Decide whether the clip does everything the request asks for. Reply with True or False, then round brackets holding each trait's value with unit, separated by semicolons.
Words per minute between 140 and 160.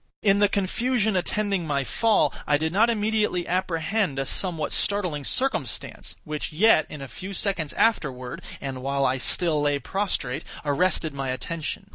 True (155 wpm)